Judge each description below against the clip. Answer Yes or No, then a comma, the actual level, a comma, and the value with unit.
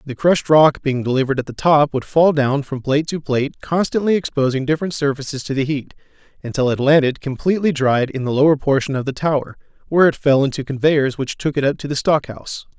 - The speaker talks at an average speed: No, fast, 220 wpm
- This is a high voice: No, medium, 145 Hz